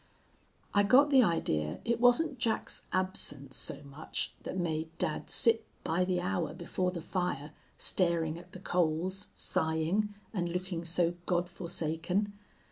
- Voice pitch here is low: No, medium, 180 Hz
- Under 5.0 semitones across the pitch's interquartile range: Yes, average, 3.5 semitones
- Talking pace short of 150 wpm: Yes, average, 140 wpm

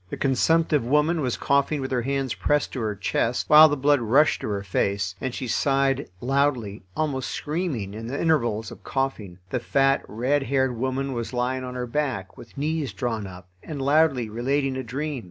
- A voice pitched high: No, low, 130 Hz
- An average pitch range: Yes, average, 3.6 semitones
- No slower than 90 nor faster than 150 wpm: No, average, 190 wpm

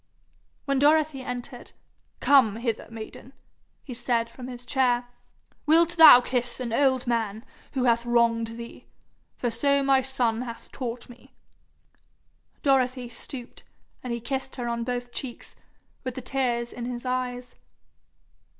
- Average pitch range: No, narrow, 2.0 semitones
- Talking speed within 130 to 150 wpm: Yes, average, 140 wpm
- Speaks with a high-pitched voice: Yes, high, 245 Hz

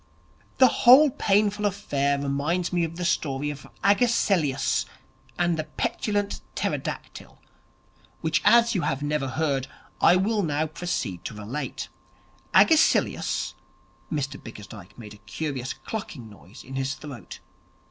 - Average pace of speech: No, slow, 130 wpm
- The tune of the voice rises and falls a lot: Yes, wide, 6.8 semitones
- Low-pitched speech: No, medium, 150 Hz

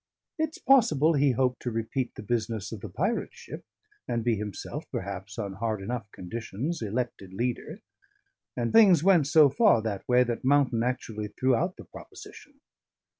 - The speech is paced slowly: No, average, 165 wpm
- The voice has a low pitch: Yes, low, 120 Hz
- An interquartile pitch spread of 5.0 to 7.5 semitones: Yes, wide, 5.4 semitones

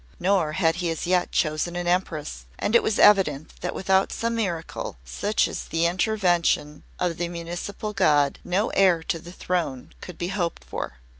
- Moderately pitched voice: Yes, medium, 175 Hz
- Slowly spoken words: No, average, 175 wpm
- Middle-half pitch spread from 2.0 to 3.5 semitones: Yes, average, 2.8 semitones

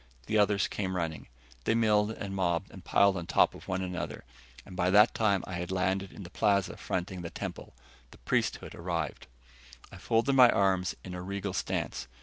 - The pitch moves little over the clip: Yes, narrow, 2.3 semitones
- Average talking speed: Yes, average, 190 wpm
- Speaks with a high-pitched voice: No, very low, 95 Hz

